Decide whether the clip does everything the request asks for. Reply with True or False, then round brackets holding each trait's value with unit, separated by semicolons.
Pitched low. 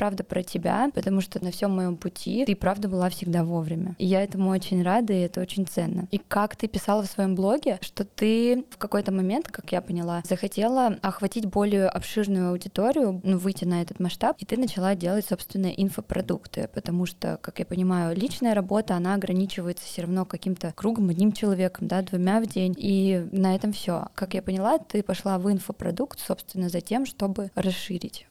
False (195 Hz)